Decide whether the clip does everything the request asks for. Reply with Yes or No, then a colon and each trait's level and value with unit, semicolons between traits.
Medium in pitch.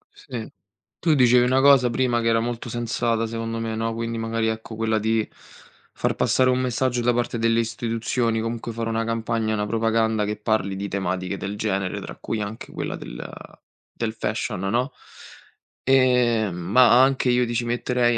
No: low, 115 Hz